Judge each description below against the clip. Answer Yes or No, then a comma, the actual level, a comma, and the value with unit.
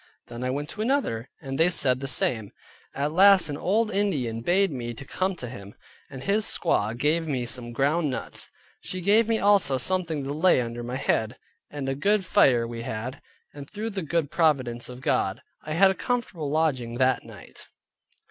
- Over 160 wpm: Yes, average, 195 wpm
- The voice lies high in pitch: No, medium, 145 Hz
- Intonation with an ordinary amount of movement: No, wide, 7.0 semitones